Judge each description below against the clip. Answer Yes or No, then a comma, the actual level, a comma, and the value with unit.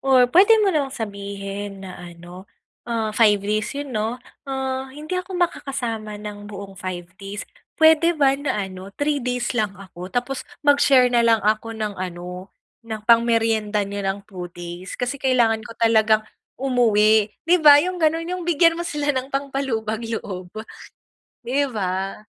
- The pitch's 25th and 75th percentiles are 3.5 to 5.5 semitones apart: Yes, average, 5.1 semitones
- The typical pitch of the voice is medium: No, high, 225 Hz